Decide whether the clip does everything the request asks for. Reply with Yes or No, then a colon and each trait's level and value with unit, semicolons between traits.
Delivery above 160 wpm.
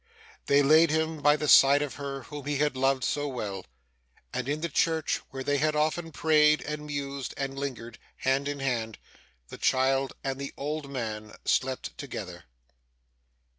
Yes: average, 170 wpm